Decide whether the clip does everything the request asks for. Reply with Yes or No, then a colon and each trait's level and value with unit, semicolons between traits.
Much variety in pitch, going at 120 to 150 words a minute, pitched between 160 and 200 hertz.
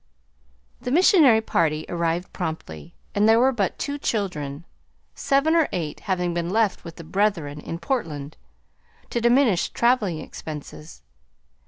Yes: wide, 6.9 semitones; slow, 135 wpm; medium, 185 Hz